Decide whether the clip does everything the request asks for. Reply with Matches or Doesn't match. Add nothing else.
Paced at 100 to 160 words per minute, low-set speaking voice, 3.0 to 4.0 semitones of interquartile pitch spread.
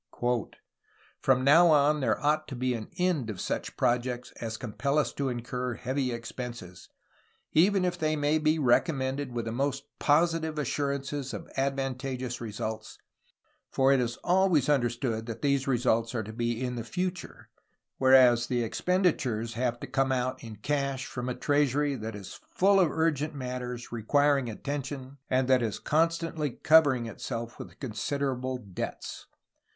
Matches